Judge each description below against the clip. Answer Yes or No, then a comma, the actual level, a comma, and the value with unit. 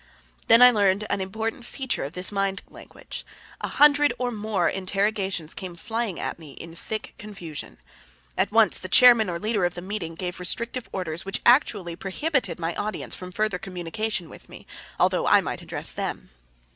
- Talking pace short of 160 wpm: No, average, 175 wpm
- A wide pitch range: No, average, 3.8 semitones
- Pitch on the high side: Yes, high, 195 Hz